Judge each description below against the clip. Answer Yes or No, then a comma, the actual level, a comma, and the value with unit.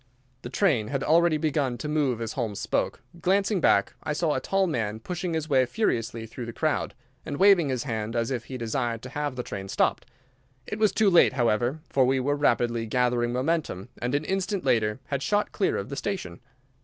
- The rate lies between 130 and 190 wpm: No, fast, 205 wpm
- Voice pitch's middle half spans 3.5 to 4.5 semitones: No, wide, 5.5 semitones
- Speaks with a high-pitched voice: No, low, 130 Hz